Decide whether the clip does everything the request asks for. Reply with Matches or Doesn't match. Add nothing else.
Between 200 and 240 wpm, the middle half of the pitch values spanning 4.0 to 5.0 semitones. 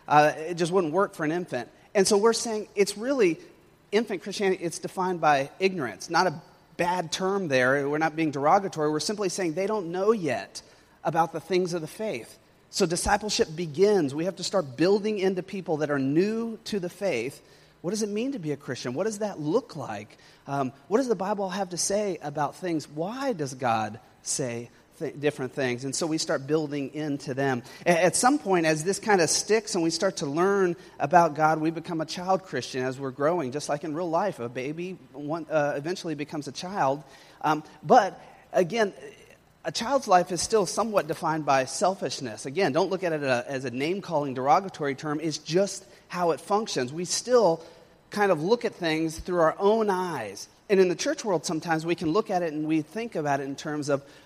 Matches